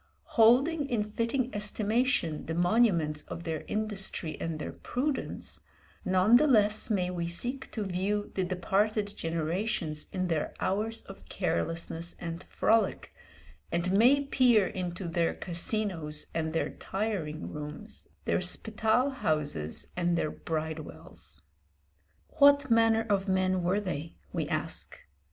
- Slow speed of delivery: Yes, slow, 130 wpm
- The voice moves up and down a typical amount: Yes, average, 5.0 semitones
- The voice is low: No, high, 190 Hz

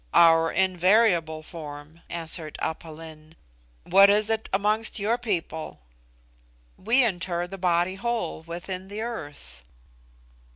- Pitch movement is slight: No, average, 4.3 semitones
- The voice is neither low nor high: Yes, medium, 175 Hz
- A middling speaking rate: No, slow, 115 wpm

